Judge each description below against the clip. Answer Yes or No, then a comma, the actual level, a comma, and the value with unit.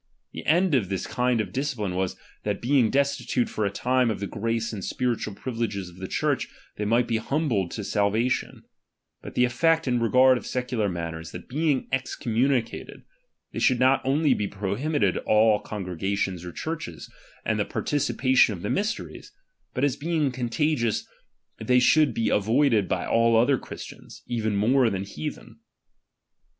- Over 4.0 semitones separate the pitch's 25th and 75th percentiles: Yes, average, 4.6 semitones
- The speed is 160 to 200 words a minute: Yes, average, 165 wpm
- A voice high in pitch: No, low, 115 Hz